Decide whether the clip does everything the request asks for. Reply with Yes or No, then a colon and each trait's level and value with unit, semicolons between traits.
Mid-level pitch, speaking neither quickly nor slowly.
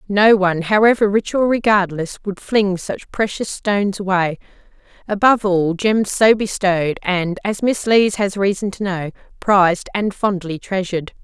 No: high, 195 Hz; average, 155 wpm